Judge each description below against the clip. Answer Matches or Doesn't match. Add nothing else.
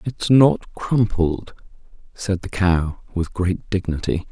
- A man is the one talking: Matches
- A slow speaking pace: Matches